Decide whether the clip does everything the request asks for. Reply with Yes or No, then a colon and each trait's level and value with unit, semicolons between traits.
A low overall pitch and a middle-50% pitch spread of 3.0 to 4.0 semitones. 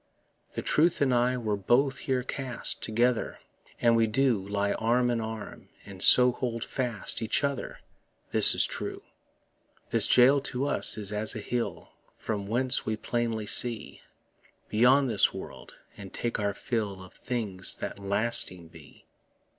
Yes: low, 115 Hz; average, 3.3 semitones